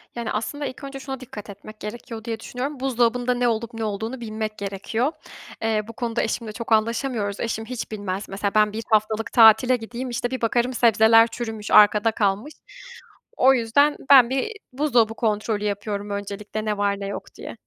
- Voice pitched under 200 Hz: No, high, 225 Hz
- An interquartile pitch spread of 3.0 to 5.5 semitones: No, narrow, 2.5 semitones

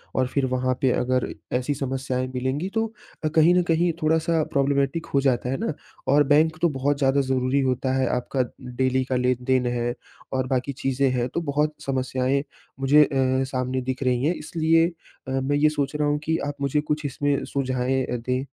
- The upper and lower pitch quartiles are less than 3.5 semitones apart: Yes, narrow, 2.6 semitones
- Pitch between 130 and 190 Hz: Yes, low, 135 Hz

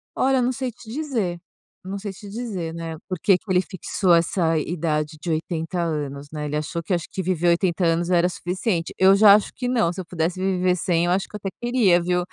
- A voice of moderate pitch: Yes, medium, 180 Hz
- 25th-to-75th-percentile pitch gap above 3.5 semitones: No, average, 2.9 semitones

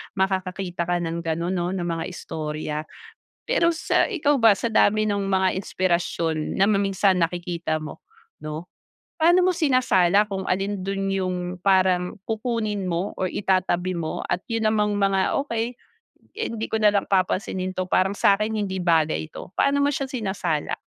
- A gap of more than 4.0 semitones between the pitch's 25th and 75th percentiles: No, average, 3.3 semitones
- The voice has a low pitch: No, high, 190 Hz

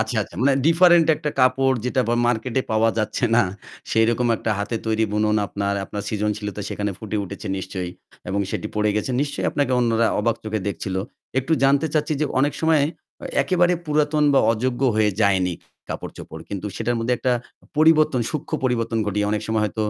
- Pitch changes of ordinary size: Yes, average, 4.7 semitones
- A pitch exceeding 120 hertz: No, low, 115 Hz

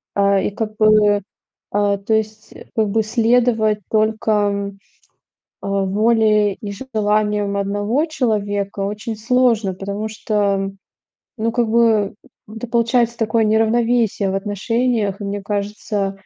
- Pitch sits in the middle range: No, high, 215 Hz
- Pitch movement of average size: No, narrow, 1.8 semitones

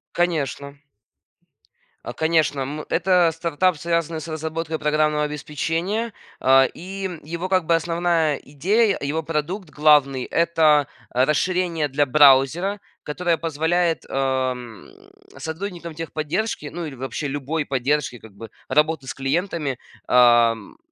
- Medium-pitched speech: Yes, medium, 155 Hz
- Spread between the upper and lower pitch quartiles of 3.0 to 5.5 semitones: Yes, average, 3.4 semitones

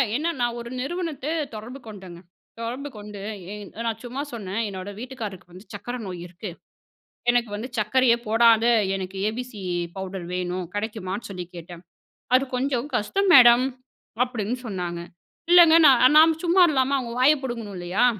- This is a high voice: Yes, high, 230 Hz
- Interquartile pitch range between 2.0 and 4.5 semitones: No, average, 4.9 semitones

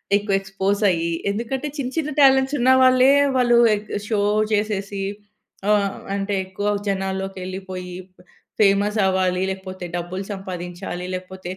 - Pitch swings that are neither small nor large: No, narrow, 2.2 semitones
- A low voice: No, high, 195 Hz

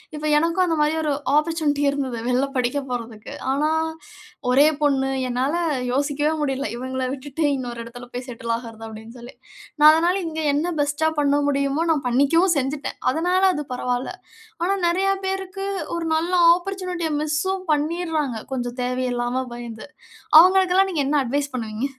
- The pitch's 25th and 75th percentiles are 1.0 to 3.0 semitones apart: No, average, 4.7 semitones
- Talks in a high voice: Yes, very high, 285 Hz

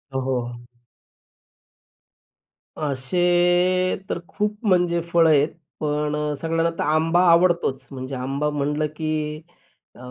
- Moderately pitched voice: Yes, medium, 155 Hz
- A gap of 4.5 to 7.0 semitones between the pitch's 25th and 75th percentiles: No, average, 3.4 semitones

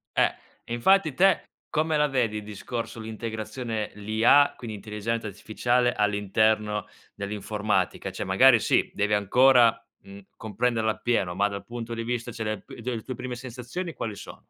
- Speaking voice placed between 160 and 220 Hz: No, low, 115 Hz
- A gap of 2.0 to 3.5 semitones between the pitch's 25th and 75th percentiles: Yes, average, 2.7 semitones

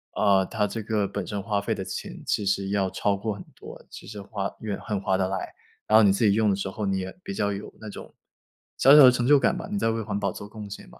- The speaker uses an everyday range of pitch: No, narrow, 1.9 semitones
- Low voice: Yes, low, 100 Hz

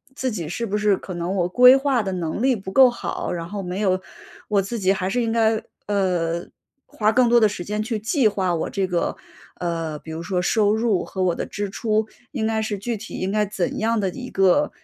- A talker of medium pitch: No, high, 205 Hz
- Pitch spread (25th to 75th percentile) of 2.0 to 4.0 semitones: Yes, average, 3.5 semitones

